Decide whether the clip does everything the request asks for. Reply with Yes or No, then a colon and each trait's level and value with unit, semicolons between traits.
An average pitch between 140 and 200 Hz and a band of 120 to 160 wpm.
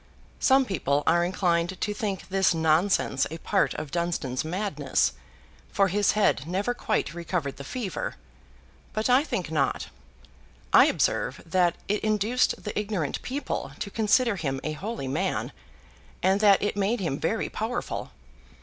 Yes: high, 190 Hz; average, 150 wpm